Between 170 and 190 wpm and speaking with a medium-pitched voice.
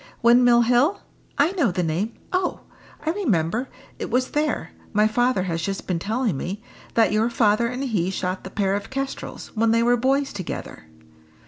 No: average, 180 wpm; high, 230 Hz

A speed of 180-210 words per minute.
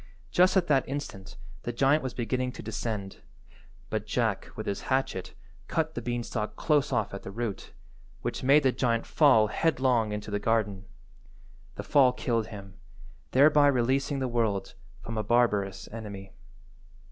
No: average, 155 wpm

